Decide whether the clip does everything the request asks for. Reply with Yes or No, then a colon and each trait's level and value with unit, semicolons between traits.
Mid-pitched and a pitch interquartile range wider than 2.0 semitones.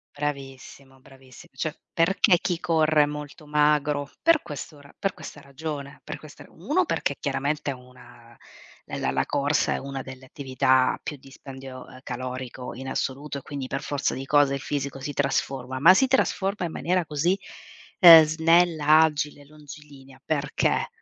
Yes: medium, 145 Hz; narrow, 2.5 semitones